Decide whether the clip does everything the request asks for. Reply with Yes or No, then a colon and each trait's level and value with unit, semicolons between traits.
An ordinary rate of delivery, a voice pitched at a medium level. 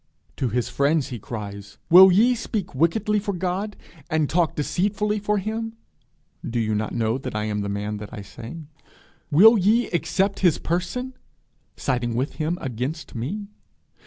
Yes: average, 160 wpm; medium, 165 Hz